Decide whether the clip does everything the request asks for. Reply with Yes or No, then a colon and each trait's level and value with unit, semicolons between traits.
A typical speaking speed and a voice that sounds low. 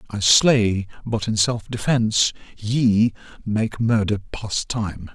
No: slow, 105 wpm; low, 110 Hz